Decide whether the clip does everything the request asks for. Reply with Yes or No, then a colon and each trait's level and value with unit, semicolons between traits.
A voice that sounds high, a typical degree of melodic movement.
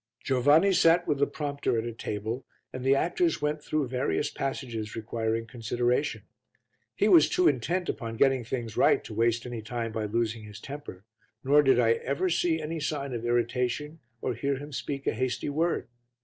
No: low, 130 Hz; average, 4.2 semitones